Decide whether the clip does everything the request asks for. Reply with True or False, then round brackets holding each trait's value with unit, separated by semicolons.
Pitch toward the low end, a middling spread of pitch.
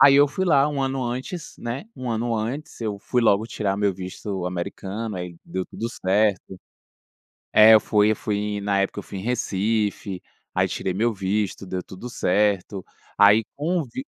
True (105 Hz; 3.9 semitones)